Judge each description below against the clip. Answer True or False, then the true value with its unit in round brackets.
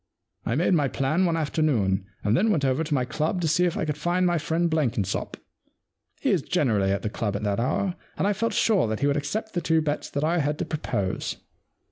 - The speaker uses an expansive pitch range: True (6.3 semitones)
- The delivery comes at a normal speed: False (235 wpm)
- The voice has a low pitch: False (150 Hz)